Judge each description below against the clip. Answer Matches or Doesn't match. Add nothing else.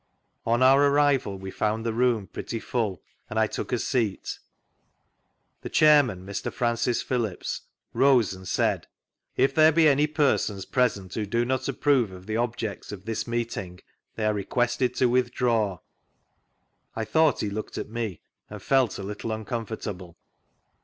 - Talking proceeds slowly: Doesn't match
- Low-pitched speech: Matches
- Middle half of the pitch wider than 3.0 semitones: Matches